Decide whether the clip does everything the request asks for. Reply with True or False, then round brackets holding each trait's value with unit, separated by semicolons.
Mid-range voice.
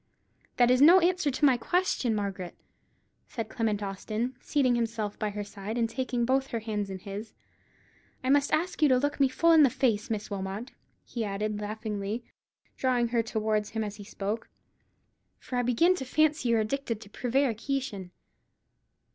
False (230 Hz)